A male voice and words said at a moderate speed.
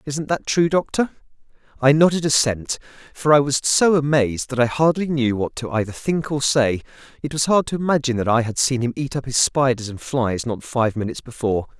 No: male; fast, 215 wpm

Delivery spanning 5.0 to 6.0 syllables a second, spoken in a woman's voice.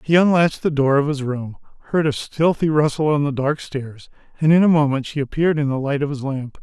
No: 5.8 syllables/s; male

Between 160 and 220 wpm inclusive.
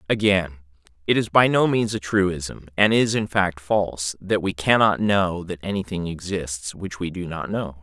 Yes: average, 190 wpm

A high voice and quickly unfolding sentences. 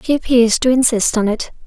Yes: high, 240 Hz; fast, 215 wpm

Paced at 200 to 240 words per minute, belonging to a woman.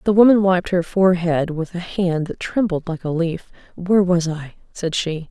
Yes: fast, 205 wpm; female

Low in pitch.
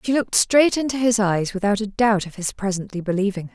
No: high, 210 Hz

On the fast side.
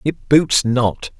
No: average, 150 wpm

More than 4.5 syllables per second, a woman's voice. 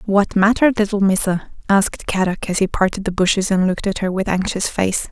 Yes: 5.8 syllables/s; female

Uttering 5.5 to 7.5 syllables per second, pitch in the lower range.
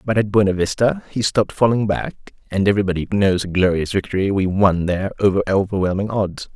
Yes: 6.0 syllables/s; low, 100 Hz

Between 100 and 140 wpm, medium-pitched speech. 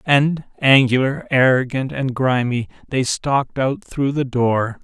No: slow, 135 wpm; low, 130 Hz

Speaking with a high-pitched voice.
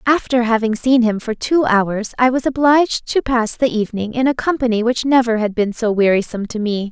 Yes: high, 235 Hz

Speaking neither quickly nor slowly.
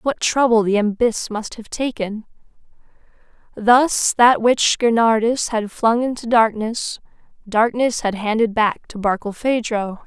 No: slow, 125 wpm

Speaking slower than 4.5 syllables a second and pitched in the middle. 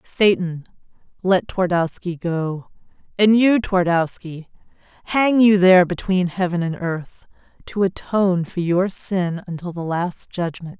Yes: 4.1 syllables/s; medium, 180 Hz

